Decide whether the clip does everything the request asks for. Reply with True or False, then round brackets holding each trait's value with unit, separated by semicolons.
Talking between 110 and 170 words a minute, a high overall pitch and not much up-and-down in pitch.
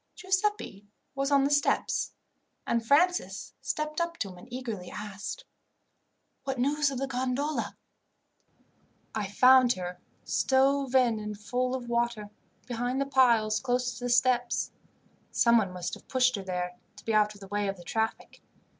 False (160 wpm; 245 Hz; 4.3 semitones)